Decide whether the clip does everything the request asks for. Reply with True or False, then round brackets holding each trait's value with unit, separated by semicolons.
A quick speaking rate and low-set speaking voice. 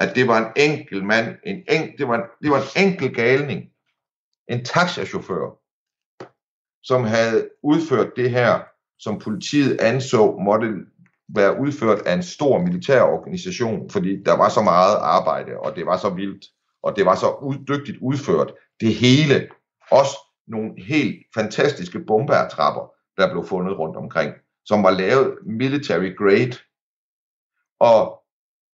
False (145 wpm; 130 Hz)